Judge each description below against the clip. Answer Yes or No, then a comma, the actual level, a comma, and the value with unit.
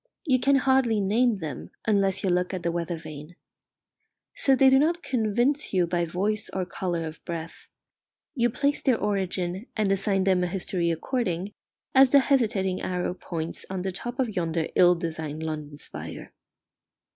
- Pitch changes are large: Yes, wide, 5.8 semitones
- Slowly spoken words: No, average, 170 wpm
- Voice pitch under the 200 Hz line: Yes, high, 190 Hz